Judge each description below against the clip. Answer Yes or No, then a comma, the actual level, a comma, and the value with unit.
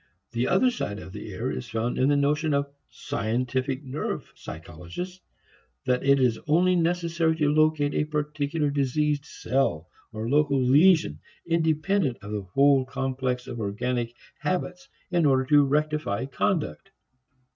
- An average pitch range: Yes, average, 3.7 semitones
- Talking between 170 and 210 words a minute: No, average, 145 wpm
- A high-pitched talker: No, medium, 140 Hz